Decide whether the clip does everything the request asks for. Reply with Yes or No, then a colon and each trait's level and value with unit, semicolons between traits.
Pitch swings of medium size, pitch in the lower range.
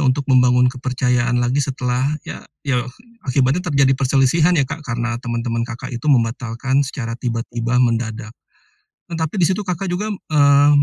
Yes: average, 3.0 semitones; low, 130 Hz